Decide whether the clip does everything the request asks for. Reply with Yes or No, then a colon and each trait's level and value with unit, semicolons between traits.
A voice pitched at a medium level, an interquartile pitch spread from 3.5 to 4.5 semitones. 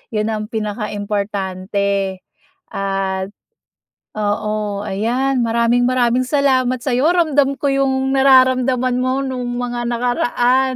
No: high, 245 Hz; average, 3.9 semitones